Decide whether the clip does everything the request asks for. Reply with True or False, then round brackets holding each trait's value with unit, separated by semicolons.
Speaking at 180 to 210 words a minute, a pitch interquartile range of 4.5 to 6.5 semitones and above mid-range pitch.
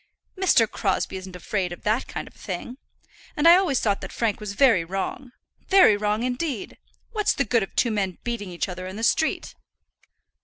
True (190 wpm; 5.1 semitones; 215 Hz)